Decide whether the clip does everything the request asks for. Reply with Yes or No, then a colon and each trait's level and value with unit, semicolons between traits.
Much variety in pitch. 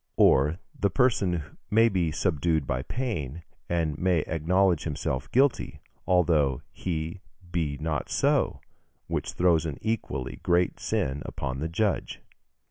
No: average, 3.9 semitones